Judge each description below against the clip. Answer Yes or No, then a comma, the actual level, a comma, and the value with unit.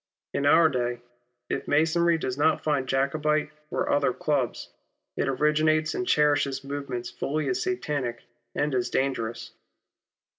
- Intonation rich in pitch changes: No, average, 3.2 semitones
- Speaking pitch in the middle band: Yes, medium, 145 Hz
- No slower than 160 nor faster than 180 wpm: No, average, 140 wpm